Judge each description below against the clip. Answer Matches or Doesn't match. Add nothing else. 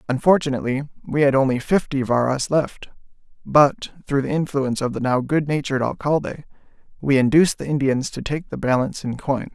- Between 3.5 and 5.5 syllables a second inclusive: Doesn't match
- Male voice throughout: Matches